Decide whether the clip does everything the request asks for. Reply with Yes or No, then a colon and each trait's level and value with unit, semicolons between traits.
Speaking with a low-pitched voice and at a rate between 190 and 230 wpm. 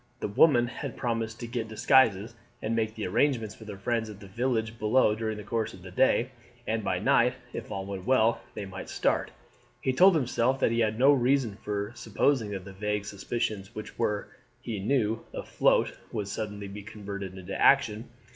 Yes: low, 110 Hz; average, 195 wpm